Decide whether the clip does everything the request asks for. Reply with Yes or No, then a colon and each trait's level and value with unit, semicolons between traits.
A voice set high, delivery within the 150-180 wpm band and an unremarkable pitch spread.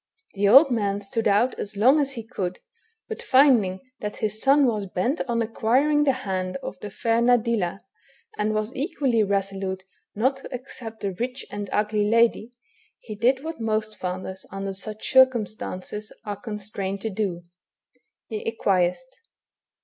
Yes: high, 215 Hz; average, 155 wpm; average, 3.8 semitones